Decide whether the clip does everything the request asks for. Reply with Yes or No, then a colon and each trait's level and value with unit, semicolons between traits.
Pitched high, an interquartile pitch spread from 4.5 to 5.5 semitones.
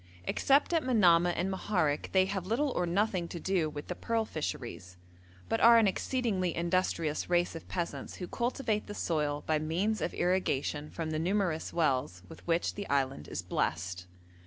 No: medium, 175 Hz; average, 4.9 semitones